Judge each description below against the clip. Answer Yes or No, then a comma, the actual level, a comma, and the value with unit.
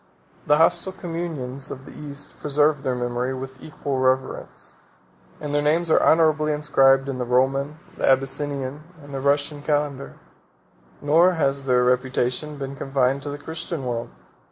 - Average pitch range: No, narrow, 2.2 semitones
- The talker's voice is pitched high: No, medium, 140 Hz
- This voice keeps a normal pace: Yes, average, 155 wpm